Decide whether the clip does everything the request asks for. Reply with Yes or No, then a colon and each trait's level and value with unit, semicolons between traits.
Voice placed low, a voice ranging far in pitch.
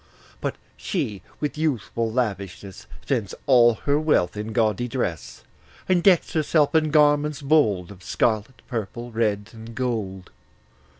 Yes: low, 120 Hz; wide, 6.0 semitones